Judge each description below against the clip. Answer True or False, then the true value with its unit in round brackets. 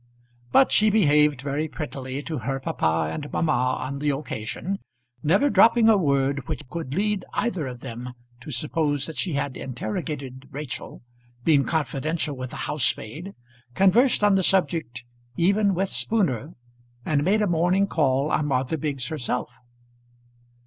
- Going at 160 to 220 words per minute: False (150 wpm)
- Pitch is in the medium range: True (150 Hz)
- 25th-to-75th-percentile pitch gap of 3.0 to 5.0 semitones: False (5.5 semitones)